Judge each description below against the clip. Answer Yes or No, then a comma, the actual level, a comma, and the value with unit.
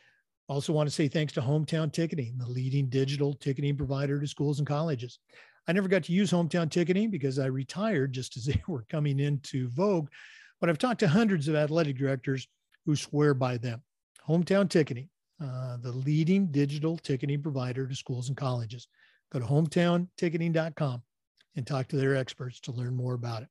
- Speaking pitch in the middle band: Yes, medium, 145 Hz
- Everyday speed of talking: Yes, average, 180 wpm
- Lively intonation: No, average, 3.8 semitones